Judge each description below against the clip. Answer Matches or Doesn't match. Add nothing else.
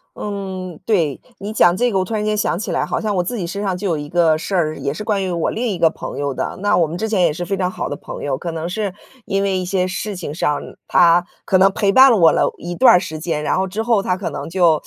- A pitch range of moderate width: Matches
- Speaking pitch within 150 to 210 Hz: Matches